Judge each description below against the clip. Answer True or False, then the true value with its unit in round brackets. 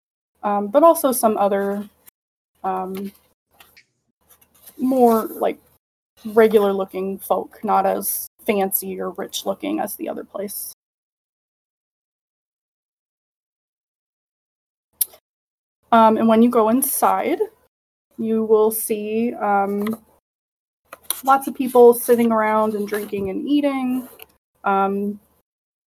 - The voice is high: True (220 Hz)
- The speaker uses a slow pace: True (95 wpm)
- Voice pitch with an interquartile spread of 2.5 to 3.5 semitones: True (3.2 semitones)